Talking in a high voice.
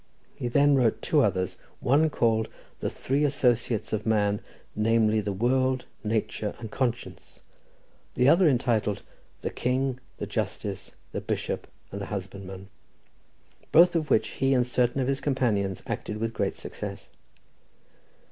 No: low, 115 Hz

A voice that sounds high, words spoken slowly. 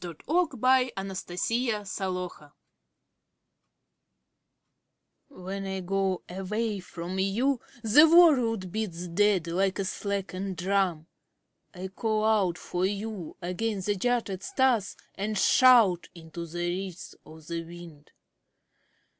Yes: high, 195 Hz; slow, 115 wpm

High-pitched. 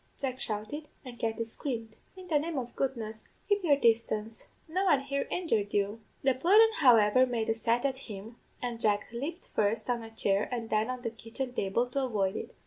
Yes: high, 235 Hz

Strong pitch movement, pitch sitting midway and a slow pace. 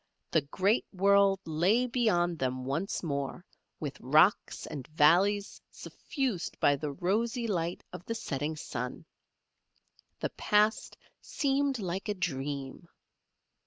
Yes: wide, 6.0 semitones; medium, 175 Hz; slow, 120 wpm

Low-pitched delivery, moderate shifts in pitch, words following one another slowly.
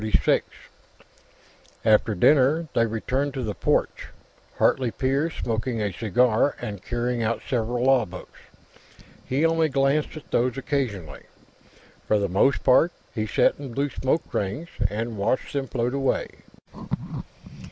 Yes: low, 125 Hz; average, 4.0 semitones; slow, 130 wpm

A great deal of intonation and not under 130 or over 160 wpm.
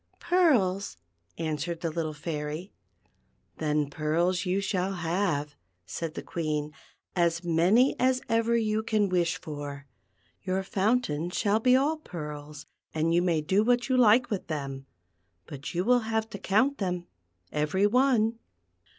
Yes: wide, 6.0 semitones; average, 140 wpm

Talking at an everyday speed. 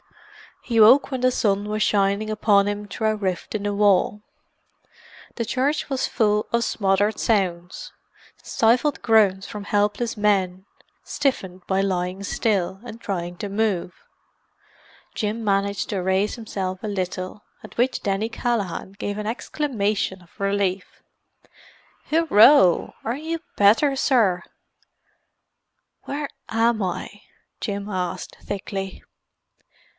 No: slow, 120 wpm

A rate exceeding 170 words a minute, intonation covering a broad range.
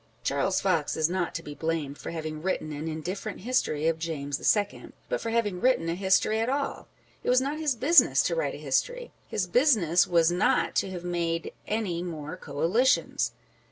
Yes: average, 195 wpm; wide, 5.8 semitones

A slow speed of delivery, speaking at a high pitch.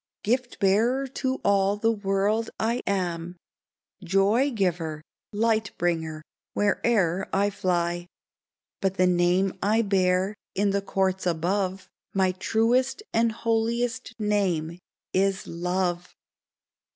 Yes: slow, 115 wpm; high, 195 Hz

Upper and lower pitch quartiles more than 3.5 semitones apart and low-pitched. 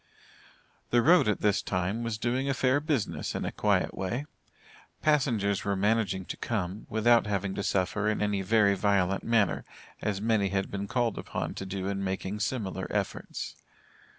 No: average, 3.1 semitones; low, 105 Hz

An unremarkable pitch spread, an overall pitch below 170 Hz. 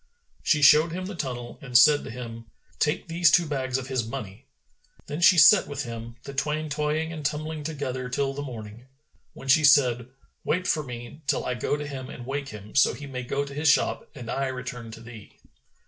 Yes: average, 3.5 semitones; low, 135 Hz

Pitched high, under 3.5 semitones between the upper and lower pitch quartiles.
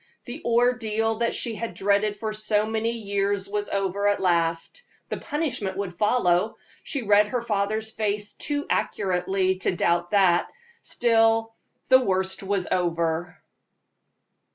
Yes: high, 205 Hz; average, 3.0 semitones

